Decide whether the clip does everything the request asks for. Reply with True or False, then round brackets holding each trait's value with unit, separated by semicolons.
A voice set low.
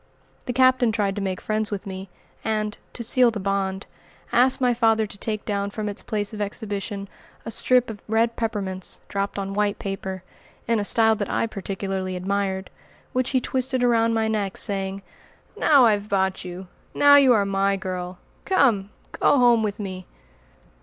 False (205 Hz)